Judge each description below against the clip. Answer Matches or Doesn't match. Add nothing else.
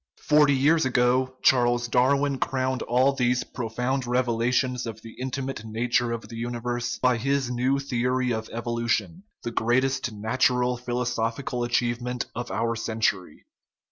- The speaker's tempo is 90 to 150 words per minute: Matches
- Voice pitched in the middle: Doesn't match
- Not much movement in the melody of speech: Matches